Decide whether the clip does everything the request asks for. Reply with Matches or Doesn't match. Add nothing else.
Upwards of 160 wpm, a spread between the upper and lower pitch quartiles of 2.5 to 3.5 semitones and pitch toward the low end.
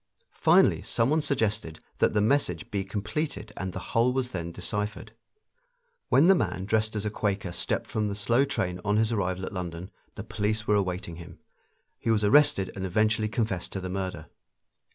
Matches